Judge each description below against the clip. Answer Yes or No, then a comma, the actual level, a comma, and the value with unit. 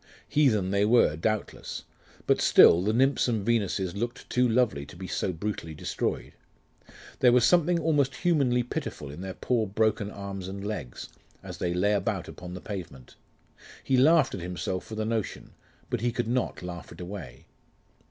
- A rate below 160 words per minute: No, average, 170 wpm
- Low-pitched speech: Yes, low, 105 Hz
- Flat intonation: No, average, 5.1 semitones